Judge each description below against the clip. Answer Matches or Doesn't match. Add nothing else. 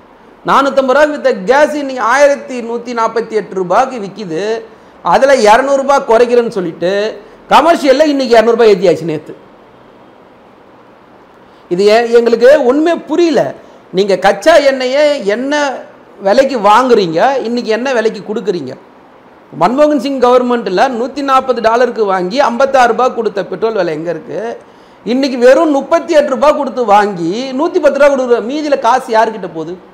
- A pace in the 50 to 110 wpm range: Doesn't match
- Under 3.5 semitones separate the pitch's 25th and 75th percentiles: Doesn't match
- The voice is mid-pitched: Doesn't match